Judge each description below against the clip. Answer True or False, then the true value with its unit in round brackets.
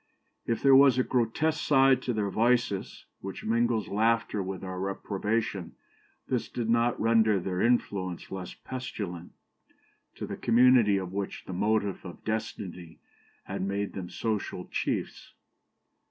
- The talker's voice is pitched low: True (110 Hz)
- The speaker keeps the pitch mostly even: False (3.6 semitones)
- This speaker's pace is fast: False (140 wpm)